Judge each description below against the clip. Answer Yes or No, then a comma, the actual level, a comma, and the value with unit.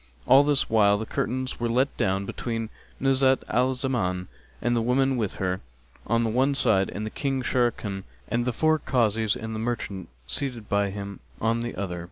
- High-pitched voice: No, low, 115 Hz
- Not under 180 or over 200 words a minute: Yes, average, 185 wpm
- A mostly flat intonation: No, average, 4.2 semitones